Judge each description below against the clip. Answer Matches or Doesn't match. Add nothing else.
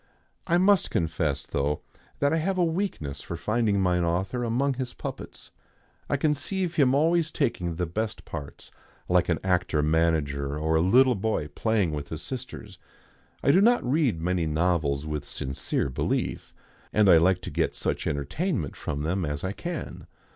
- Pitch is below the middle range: Matches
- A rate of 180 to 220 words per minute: Doesn't match